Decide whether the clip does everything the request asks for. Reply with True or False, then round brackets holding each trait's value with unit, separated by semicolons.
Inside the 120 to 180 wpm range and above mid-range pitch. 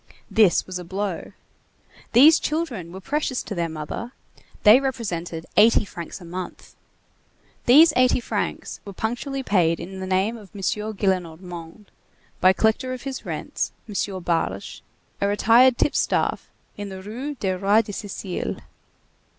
True (145 wpm; 205 Hz)